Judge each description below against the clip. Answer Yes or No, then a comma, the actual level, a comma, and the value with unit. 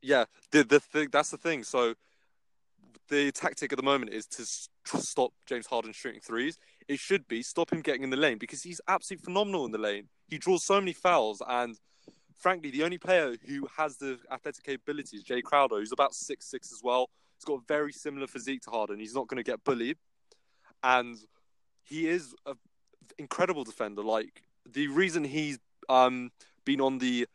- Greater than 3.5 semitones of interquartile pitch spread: Yes, average, 4.6 semitones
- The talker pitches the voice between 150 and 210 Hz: No, medium, 140 Hz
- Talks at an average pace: Yes, average, 195 wpm